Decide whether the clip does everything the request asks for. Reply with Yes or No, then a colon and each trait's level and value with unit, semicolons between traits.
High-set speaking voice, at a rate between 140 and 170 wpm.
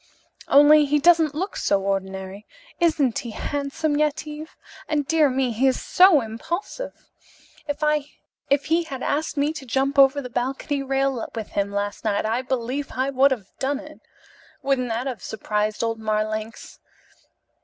Yes: very high, 270 Hz; average, 155 wpm